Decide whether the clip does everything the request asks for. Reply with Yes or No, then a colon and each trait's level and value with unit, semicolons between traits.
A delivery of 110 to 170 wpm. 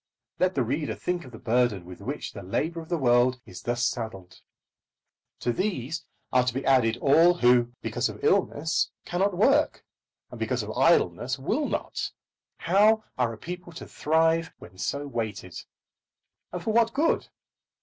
Yes: average, 165 wpm